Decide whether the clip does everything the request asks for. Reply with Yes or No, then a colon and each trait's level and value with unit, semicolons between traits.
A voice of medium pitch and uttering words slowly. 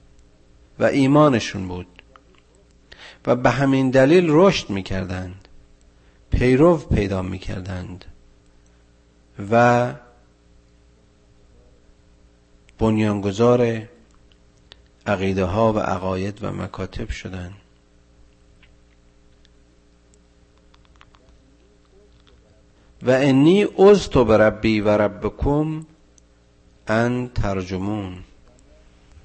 No: very low, 90 Hz; slow, 60 wpm